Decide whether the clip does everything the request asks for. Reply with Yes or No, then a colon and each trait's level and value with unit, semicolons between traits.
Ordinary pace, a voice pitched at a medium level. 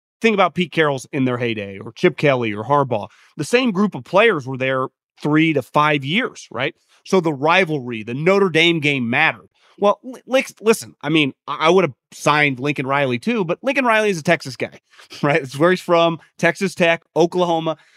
Yes: average, 195 wpm; medium, 160 Hz